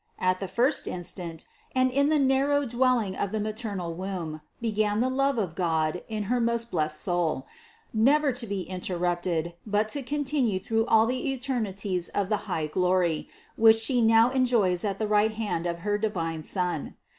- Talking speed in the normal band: Yes, average, 180 wpm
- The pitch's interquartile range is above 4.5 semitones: Yes, average, 5.1 semitones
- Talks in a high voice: Yes, high, 210 Hz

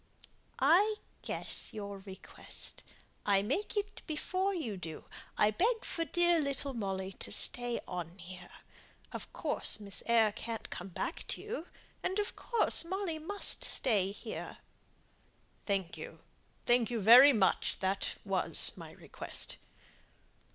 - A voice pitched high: Yes, high, 235 Hz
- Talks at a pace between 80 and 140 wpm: Yes, slow, 135 wpm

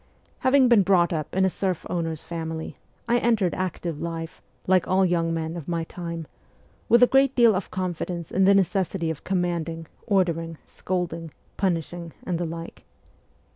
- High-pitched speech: No, medium, 175 Hz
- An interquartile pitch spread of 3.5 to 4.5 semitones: No, narrow, 2.4 semitones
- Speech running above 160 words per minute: Yes, average, 170 wpm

